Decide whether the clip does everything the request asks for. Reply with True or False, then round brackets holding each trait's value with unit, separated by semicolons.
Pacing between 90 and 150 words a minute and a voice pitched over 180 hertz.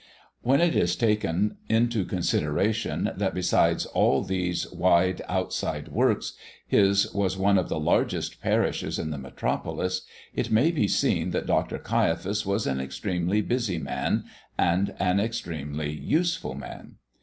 False (140 wpm; 95 Hz)